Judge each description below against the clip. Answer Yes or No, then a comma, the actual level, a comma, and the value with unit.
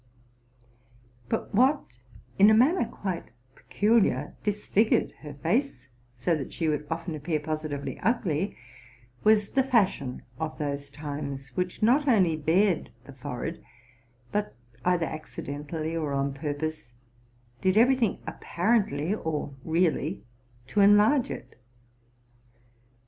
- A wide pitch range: Yes, wide, 6.2 semitones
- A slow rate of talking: Yes, slow, 120 wpm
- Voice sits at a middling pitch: Yes, medium, 165 Hz